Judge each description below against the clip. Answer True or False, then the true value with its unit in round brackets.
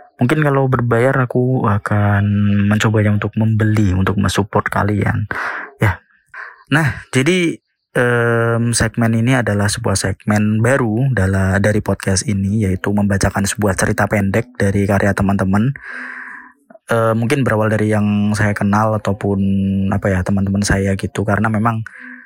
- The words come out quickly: False (130 wpm)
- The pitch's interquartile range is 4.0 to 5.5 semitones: False (2.5 semitones)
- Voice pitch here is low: True (105 Hz)